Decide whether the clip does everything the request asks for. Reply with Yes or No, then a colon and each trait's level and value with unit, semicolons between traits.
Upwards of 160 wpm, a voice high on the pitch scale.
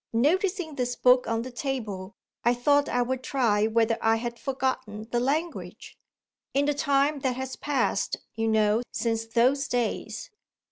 No: average, 155 wpm; high, 245 Hz